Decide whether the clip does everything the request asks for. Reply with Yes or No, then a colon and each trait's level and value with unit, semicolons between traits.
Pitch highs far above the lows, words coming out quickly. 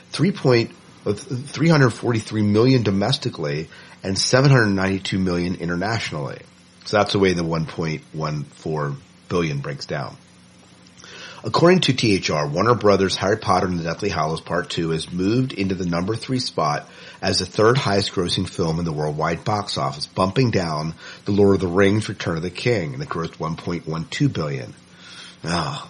No: wide, 6.5 semitones; average, 155 wpm